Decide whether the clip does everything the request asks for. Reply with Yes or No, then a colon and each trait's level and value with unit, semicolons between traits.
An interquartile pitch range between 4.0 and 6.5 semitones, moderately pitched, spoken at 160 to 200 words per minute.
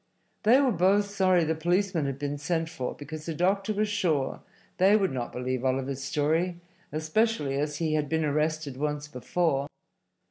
Yes: average, 4.4 semitones; medium, 155 Hz; average, 170 wpm